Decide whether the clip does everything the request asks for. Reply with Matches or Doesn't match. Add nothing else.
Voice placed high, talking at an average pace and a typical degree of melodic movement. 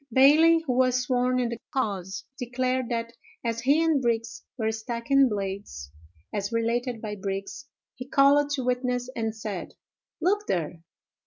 Matches